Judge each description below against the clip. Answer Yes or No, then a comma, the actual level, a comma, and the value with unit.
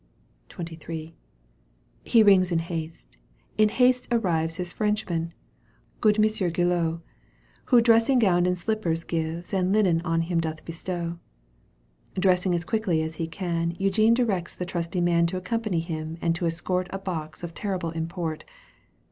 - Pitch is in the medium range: Yes, medium, 175 Hz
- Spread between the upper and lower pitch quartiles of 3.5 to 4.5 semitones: No, average, 2.9 semitones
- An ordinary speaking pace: Yes, average, 150 wpm